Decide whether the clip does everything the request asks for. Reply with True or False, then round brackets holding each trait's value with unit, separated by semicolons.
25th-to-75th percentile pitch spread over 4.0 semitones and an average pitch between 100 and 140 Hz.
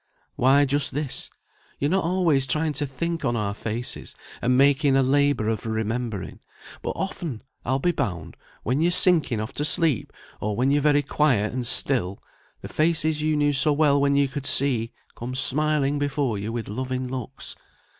False (3.7 semitones; 135 Hz)